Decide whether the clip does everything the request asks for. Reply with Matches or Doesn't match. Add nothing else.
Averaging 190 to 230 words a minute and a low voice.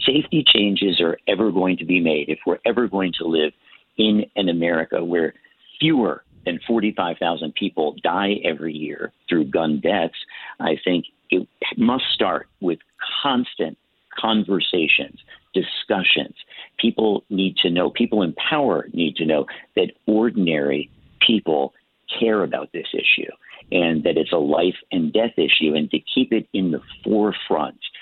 Doesn't match